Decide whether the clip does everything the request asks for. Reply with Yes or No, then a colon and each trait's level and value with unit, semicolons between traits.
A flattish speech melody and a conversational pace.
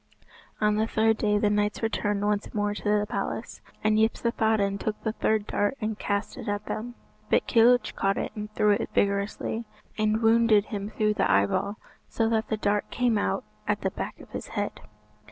Yes: narrow, 1.3 semitones; average, 190 wpm